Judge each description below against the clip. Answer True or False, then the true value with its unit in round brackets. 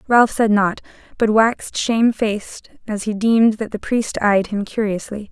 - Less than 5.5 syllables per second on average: True (4.8 syllables/s)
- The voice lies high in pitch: True (215 Hz)